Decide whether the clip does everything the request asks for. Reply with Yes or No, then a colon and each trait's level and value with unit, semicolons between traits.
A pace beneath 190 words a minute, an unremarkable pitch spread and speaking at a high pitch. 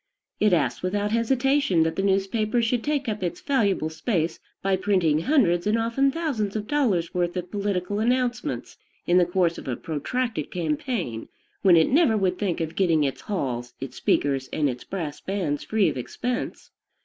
No: average, 175 wpm; wide, 5.8 semitones; high, 195 Hz